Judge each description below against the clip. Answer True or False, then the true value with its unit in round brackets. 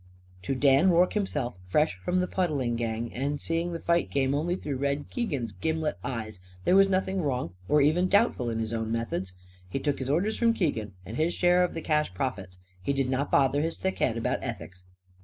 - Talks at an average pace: False (210 wpm)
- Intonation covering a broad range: True (6.8 semitones)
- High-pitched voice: False (140 Hz)